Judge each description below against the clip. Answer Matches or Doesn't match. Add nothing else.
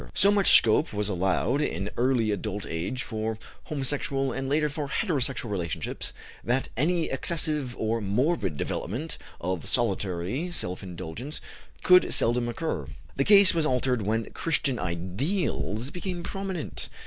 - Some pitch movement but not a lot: Doesn't match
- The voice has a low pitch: Matches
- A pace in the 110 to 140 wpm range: Matches